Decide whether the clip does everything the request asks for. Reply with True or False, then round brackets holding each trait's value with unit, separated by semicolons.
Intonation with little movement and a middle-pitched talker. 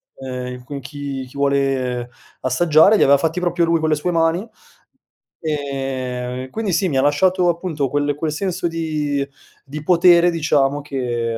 False (3.9 semitones; 145 Hz)